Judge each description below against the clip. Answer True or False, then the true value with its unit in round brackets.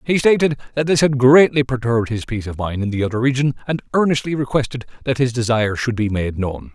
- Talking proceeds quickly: True (220 wpm)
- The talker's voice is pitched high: False (125 Hz)